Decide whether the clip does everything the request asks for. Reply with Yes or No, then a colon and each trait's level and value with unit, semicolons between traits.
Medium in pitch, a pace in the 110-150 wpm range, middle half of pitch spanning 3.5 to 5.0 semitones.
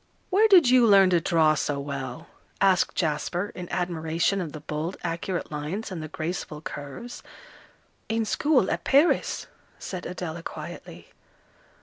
Yes: medium, 175 Hz; average, 140 wpm; average, 4.4 semitones